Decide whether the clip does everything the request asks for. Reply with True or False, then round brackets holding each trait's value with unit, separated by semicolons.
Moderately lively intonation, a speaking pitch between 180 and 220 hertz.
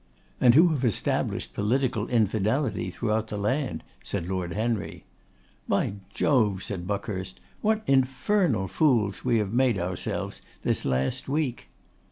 False (5.0 semitones; 110 Hz)